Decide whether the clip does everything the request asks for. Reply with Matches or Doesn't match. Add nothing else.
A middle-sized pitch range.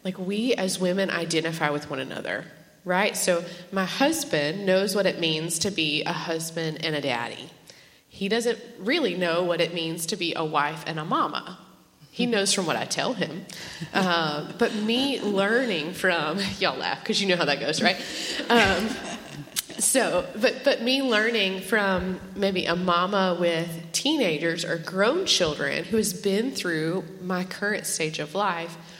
Matches